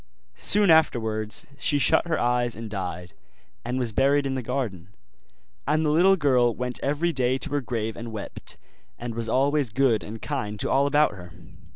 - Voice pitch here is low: Yes, low, 125 Hz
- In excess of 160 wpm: Yes, average, 185 wpm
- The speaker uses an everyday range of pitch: Yes, average, 4.4 semitones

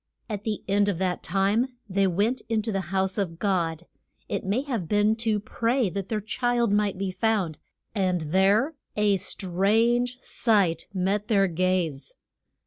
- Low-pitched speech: No, high, 200 Hz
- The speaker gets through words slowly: No, average, 160 wpm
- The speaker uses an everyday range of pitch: Yes, average, 3.0 semitones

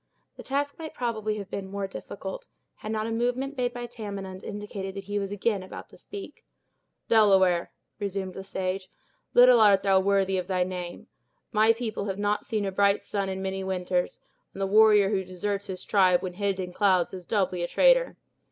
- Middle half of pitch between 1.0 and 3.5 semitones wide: Yes, narrow, 2.4 semitones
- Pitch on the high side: Yes, high, 200 Hz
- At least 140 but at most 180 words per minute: No, average, 195 wpm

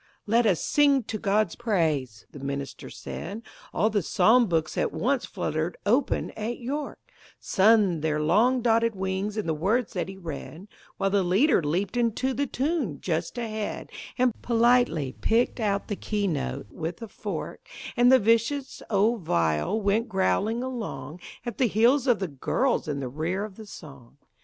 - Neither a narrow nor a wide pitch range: No, wide, 6.2 semitones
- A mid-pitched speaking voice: No, high, 205 Hz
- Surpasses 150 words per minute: Yes, average, 170 wpm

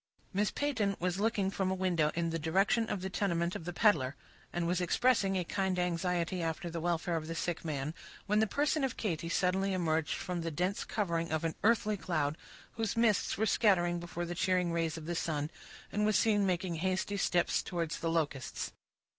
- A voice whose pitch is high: No, medium, 180 Hz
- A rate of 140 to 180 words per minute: No, average, 200 wpm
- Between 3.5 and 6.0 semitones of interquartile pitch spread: No, average, 3.0 semitones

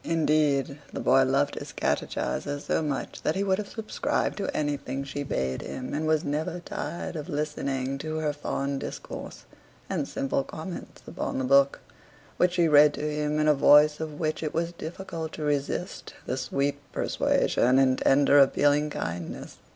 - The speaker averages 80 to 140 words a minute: No, average, 170 wpm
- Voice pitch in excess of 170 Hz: No, medium, 145 Hz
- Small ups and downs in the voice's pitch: Yes, narrow, 2.3 semitones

